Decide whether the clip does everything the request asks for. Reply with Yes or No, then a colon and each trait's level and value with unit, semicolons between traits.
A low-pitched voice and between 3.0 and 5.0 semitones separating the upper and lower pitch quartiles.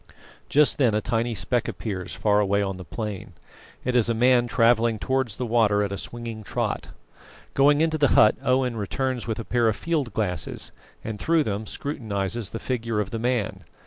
Yes: low, 115 Hz; average, 3.3 semitones